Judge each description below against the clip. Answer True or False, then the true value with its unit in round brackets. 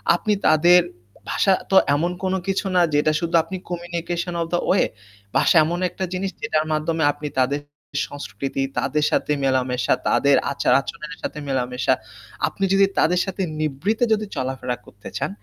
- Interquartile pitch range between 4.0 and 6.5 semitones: True (4.6 semitones)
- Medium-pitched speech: True (155 Hz)